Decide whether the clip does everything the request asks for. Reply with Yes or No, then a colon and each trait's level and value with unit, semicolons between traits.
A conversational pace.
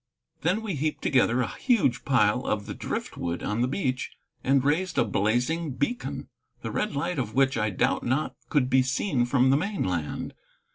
Yes: average, 180 wpm